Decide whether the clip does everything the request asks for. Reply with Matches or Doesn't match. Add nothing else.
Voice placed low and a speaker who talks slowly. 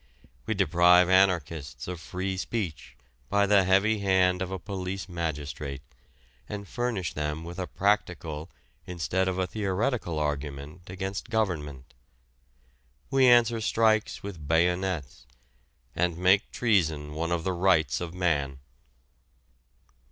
Matches